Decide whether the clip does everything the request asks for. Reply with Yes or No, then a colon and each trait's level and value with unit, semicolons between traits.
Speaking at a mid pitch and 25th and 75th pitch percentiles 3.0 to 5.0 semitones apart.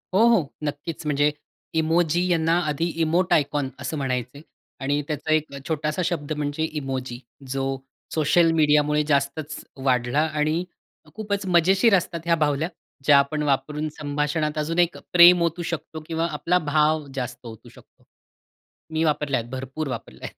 No: medium, 150 Hz; narrow, 2.6 semitones